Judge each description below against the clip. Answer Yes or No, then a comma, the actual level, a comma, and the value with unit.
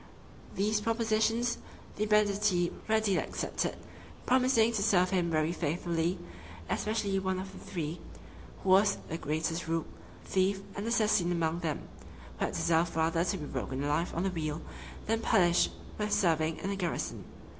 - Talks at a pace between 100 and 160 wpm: Yes, average, 155 wpm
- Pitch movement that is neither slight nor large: Yes, average, 4.3 semitones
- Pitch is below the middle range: No, medium, 185 Hz